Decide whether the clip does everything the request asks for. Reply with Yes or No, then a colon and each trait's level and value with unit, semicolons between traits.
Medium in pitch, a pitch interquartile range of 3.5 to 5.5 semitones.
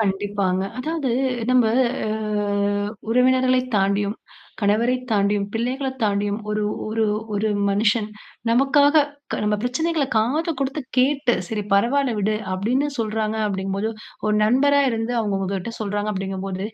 No: high, 220 Hz; average, 4.0 semitones